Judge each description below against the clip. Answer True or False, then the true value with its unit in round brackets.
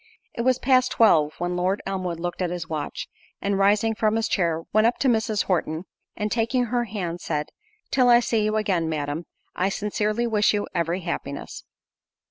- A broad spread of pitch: False (4.6 semitones)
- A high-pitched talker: True (200 Hz)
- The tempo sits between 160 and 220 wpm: True (185 wpm)